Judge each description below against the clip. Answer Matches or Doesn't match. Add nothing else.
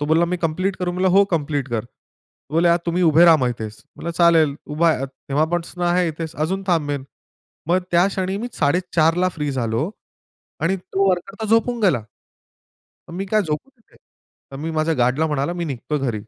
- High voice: Doesn't match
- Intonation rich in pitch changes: Doesn't match